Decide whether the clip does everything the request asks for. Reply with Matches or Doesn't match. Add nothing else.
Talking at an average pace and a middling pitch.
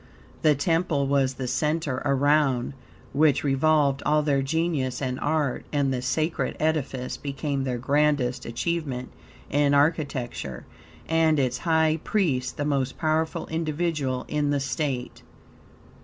Doesn't match